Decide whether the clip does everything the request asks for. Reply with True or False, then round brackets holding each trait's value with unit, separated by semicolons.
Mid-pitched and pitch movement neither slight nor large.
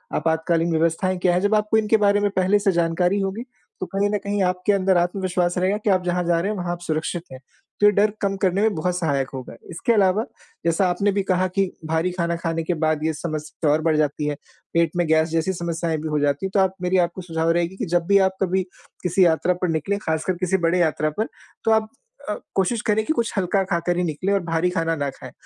True (180 Hz; 3.0 semitones)